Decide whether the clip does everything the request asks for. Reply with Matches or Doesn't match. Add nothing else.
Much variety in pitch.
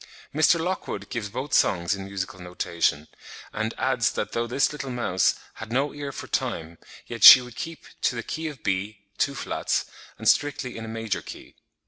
Matches